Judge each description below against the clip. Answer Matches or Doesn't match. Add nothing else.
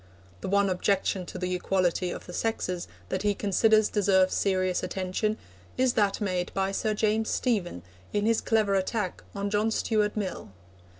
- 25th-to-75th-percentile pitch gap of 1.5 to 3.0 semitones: Matches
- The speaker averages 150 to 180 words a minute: Matches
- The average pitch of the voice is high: Matches